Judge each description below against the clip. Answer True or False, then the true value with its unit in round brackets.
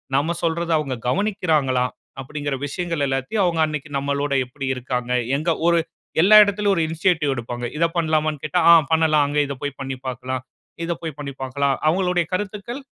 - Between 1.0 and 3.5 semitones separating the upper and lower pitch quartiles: False (3.9 semitones)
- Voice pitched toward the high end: False (155 Hz)